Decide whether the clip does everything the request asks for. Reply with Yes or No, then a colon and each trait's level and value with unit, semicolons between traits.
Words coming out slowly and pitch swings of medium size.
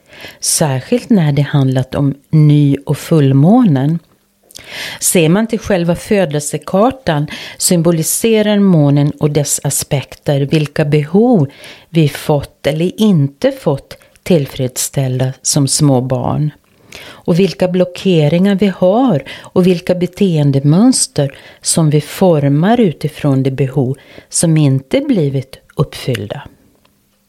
Yes: slow, 105 wpm; average, 4.6 semitones